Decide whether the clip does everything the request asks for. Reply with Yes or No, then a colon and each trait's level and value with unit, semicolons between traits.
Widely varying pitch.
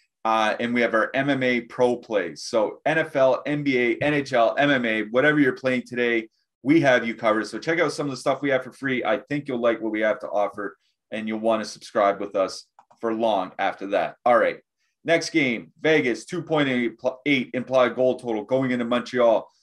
No: average, 3.8 semitones